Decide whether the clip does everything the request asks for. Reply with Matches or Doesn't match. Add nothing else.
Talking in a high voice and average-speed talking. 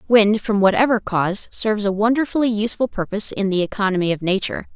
Matches